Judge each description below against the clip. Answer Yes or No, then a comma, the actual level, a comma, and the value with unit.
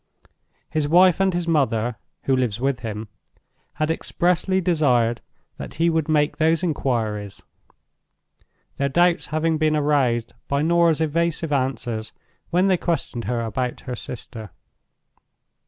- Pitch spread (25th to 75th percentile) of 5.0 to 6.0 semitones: Yes, wide, 5.5 semitones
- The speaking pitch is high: No, medium, 150 Hz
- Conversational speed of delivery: No, slow, 130 wpm